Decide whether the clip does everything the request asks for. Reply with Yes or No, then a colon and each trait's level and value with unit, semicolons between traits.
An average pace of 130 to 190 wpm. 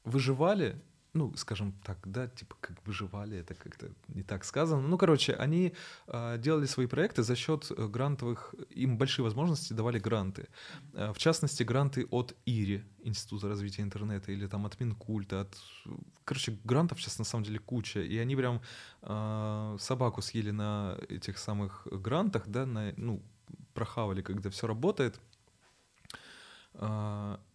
Yes: average, 145 wpm